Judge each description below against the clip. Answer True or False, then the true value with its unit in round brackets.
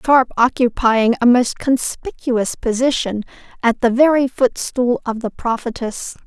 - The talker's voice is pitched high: True (245 Hz)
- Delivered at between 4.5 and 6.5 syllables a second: False (4.2 syllables/s)